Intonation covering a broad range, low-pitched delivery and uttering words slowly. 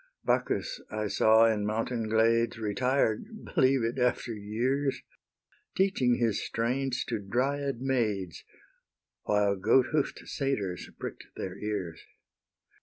No: average, 3.9 semitones; low, 115 Hz; slow, 110 wpm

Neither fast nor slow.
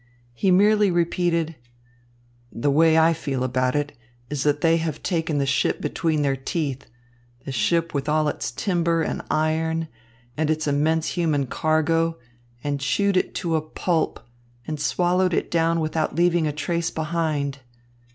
Yes: average, 155 wpm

